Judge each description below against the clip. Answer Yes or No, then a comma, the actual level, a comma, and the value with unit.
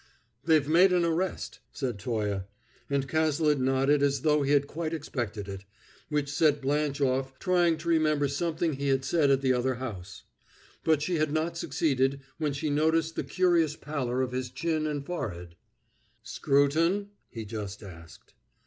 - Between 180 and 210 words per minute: No, average, 165 wpm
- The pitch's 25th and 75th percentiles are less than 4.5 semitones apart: Yes, average, 3.4 semitones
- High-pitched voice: No, medium, 145 Hz